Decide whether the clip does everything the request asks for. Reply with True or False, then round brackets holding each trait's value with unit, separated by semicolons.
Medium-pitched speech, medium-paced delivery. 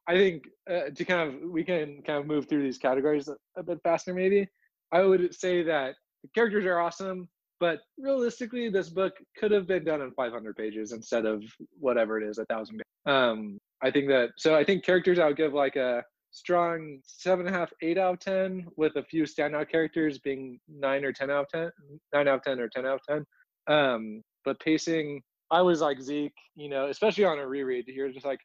False (155 Hz; 220 wpm)